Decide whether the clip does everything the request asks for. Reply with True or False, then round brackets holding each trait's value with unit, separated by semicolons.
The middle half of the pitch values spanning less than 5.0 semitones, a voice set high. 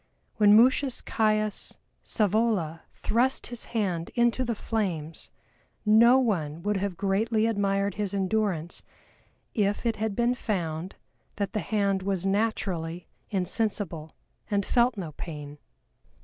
True (3.6 semitones; 205 Hz)